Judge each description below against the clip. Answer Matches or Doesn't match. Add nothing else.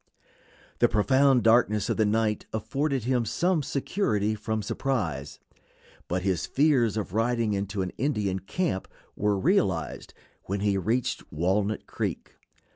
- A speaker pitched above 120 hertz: Doesn't match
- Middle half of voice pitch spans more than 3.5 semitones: Matches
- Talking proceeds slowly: Matches